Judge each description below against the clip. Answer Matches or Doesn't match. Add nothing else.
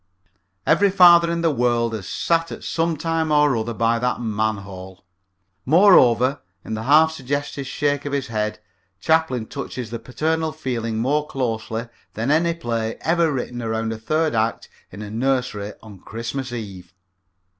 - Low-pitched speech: Matches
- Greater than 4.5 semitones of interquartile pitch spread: Matches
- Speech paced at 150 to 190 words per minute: Matches